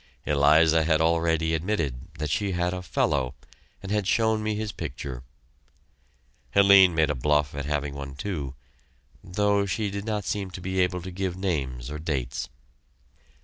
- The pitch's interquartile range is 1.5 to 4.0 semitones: No, average, 5.1 semitones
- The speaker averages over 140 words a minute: Yes, average, 150 wpm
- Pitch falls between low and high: No, very low, 85 Hz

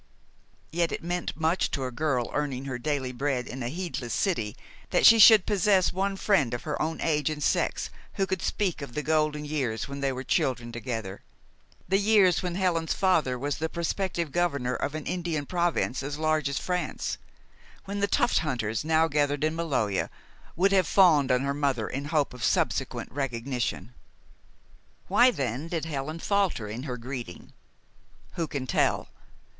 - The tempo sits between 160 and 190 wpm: Yes, average, 175 wpm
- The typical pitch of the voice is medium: Yes, medium, 150 Hz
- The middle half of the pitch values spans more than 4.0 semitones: Yes, average, 5.1 semitones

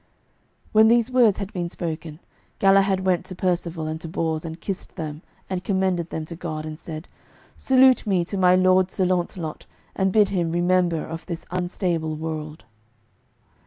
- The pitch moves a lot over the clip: No, average, 2.8 semitones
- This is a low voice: No, medium, 180 Hz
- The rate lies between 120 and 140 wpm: No, average, 165 wpm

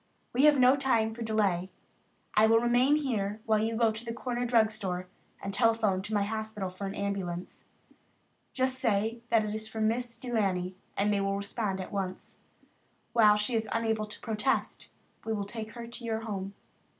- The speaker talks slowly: No, average, 190 wpm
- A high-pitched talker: Yes, high, 220 Hz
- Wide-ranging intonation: No, narrow, 2.6 semitones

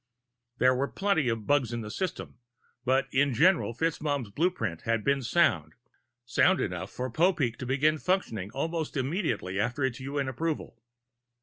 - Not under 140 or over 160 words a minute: Yes, average, 150 wpm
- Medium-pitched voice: No, low, 130 Hz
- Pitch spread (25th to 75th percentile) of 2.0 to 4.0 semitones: No, wide, 5.5 semitones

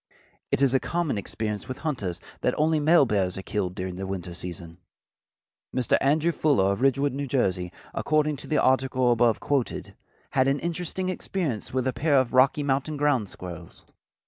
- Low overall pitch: Yes, low, 130 Hz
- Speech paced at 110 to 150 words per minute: No, average, 175 wpm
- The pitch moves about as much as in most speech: No, wide, 6.8 semitones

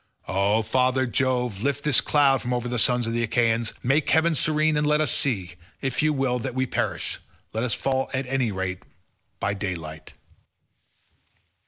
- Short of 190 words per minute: Yes, average, 175 wpm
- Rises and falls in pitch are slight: No, average, 3.4 semitones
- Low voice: Yes, low, 125 Hz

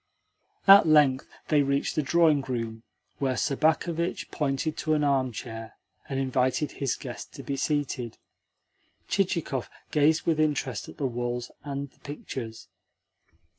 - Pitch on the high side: No, medium, 140 Hz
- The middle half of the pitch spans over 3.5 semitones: No, average, 3.1 semitones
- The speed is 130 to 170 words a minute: Yes, slow, 135 wpm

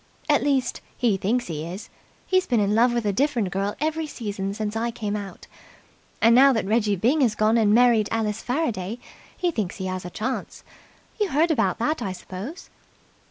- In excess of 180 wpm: Yes, average, 195 wpm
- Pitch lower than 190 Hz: No, high, 225 Hz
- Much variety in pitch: No, average, 4.6 semitones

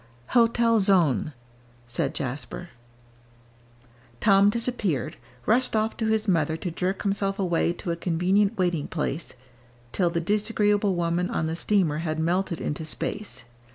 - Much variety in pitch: No, average, 4.1 semitones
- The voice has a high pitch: No, medium, 180 Hz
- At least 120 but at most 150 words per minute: Yes, slow, 135 wpm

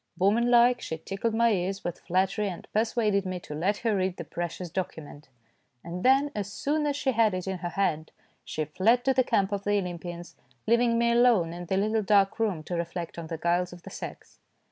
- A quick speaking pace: Yes, fast, 220 wpm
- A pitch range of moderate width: Yes, average, 4.8 semitones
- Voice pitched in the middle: No, high, 195 Hz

